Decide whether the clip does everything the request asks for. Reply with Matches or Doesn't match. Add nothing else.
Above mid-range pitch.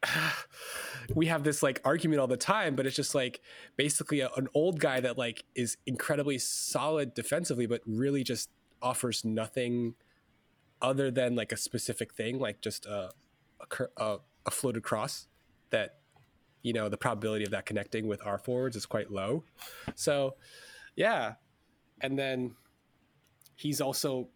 Doesn't match